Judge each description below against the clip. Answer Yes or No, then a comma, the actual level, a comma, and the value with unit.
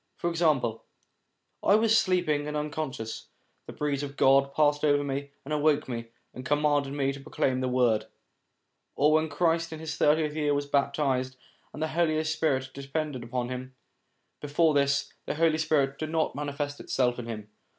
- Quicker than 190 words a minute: No, average, 180 wpm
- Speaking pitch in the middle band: Yes, medium, 145 Hz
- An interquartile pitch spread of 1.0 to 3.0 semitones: Yes, narrow, 2.6 semitones